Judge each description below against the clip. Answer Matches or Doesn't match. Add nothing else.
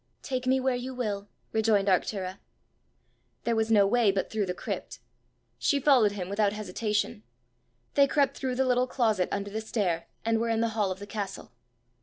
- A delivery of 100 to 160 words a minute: Doesn't match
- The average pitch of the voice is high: Matches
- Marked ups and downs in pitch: Doesn't match